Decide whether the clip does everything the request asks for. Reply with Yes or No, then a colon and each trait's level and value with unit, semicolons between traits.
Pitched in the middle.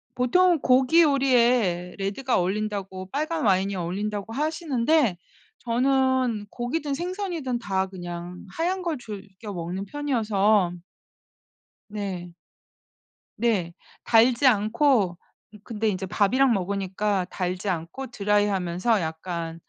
No: high, 210 Hz